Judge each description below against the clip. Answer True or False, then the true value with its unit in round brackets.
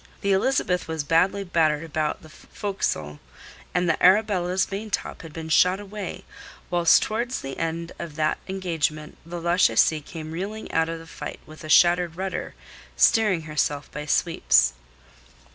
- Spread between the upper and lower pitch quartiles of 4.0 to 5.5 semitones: False (3.3 semitones)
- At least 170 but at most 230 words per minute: False (150 wpm)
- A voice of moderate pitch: True (170 Hz)